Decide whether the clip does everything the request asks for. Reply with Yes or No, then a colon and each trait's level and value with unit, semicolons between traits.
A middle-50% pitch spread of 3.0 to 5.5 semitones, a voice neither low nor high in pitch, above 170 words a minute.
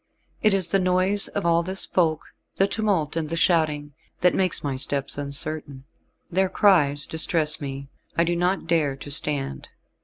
No: average, 4.2 semitones; medium, 165 Hz; average, 165 wpm